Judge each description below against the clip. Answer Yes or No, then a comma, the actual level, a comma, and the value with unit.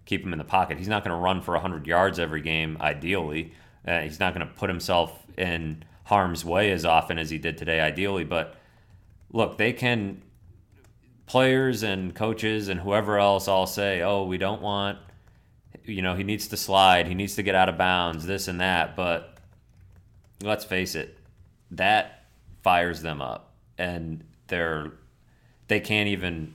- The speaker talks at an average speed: Yes, average, 175 wpm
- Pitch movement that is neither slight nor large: Yes, average, 3.2 semitones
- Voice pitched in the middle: No, very low, 95 Hz